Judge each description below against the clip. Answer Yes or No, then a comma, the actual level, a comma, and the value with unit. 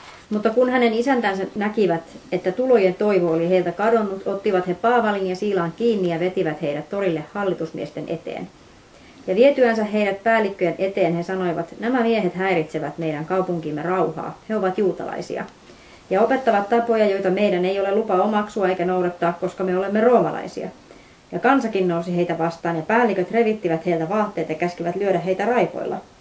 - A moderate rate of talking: No, fast, 160 wpm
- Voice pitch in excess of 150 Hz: Yes, high, 190 Hz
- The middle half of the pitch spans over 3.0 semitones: Yes, average, 3.6 semitones